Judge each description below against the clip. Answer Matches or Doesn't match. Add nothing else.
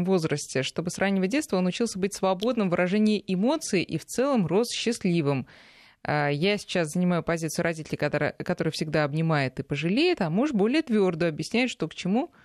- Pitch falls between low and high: Matches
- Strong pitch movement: Doesn't match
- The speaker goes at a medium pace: Doesn't match